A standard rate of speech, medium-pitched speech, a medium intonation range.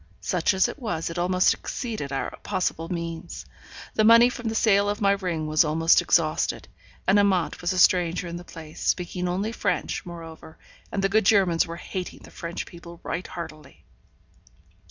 Yes: average, 175 wpm; medium, 180 Hz; average, 3.2 semitones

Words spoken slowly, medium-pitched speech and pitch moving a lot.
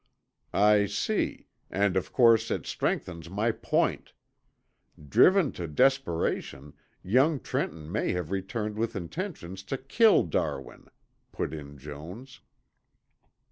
No: slow, 110 wpm; low, 100 Hz; wide, 7.5 semitones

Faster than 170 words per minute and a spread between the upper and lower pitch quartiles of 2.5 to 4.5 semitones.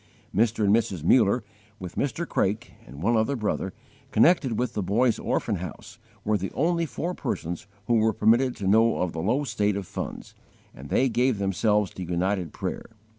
Yes: average, 180 wpm; average, 4.1 semitones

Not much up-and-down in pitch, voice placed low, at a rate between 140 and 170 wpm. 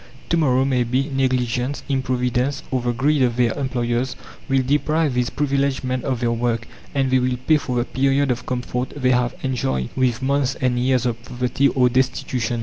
No: narrow, 1.6 semitones; low, 130 Hz; average, 185 wpm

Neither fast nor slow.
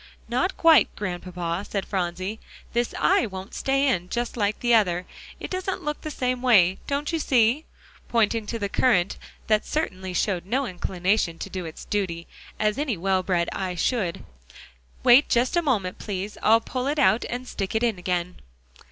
Yes: average, 180 wpm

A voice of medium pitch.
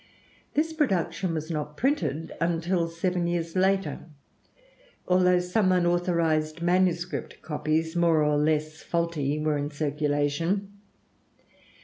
Yes: medium, 170 Hz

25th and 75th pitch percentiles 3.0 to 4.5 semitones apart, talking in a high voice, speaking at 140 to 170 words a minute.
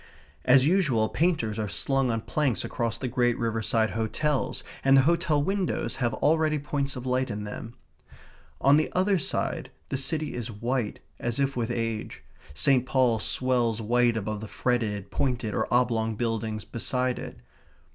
No: average, 3.5 semitones; low, 125 Hz; average, 160 wpm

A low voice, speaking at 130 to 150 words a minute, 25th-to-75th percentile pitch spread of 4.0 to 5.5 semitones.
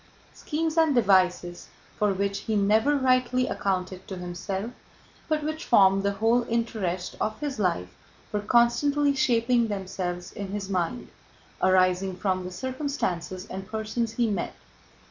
No: high, 205 Hz; average, 140 wpm; average, 4.8 semitones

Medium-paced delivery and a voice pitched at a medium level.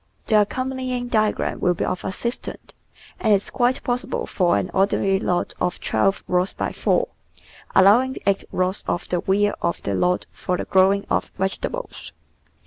No: average, 160 wpm; high, 195 Hz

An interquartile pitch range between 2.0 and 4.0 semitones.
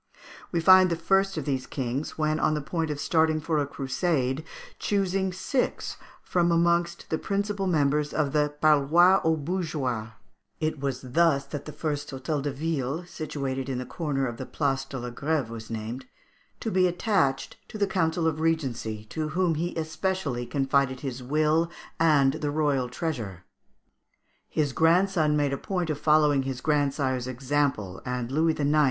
Yes: average, 3.5 semitones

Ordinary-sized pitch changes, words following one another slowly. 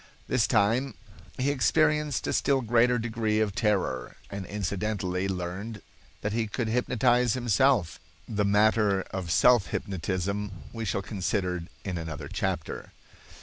Yes: average, 4.0 semitones; slow, 130 wpm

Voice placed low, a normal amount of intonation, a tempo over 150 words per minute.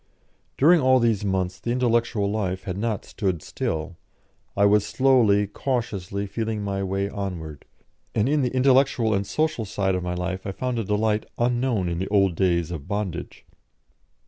Yes: low, 100 Hz; average, 3.9 semitones; average, 170 wpm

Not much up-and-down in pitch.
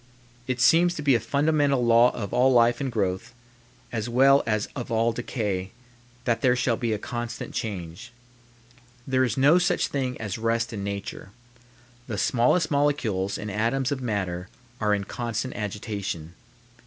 No: average, 3.9 semitones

